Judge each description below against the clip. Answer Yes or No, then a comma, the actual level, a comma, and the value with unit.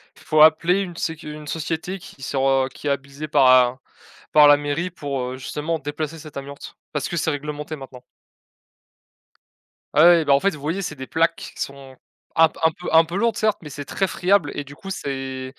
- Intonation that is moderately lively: Yes, average, 3.0 semitones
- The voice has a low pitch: No, medium, 150 Hz